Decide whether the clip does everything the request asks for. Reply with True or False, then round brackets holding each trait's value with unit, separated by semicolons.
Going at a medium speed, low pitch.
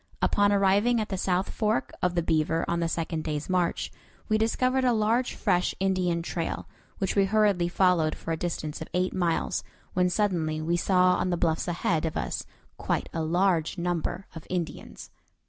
False (180 wpm; 180 Hz)